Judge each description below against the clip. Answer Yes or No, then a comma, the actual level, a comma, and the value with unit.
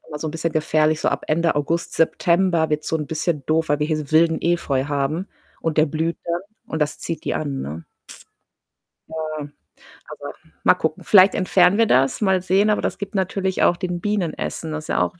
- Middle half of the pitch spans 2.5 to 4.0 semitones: Yes, average, 2.8 semitones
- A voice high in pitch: No, medium, 160 Hz